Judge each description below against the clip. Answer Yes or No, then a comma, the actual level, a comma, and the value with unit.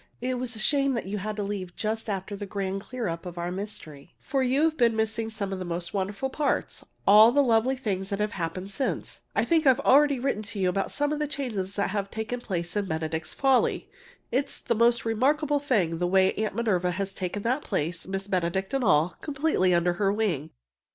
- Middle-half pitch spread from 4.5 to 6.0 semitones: Yes, average, 5.3 semitones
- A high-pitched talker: Yes, high, 210 Hz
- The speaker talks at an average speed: No, fast, 215 wpm